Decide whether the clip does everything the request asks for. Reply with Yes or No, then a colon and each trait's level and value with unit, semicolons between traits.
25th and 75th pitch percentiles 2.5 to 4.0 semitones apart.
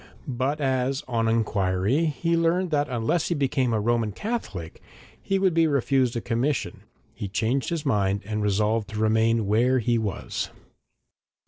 No: average, 5.0 semitones